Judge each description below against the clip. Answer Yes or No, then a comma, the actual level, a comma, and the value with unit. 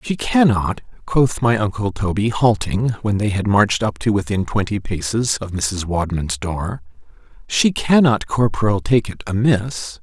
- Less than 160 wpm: Yes, average, 150 wpm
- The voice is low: Yes, low, 105 Hz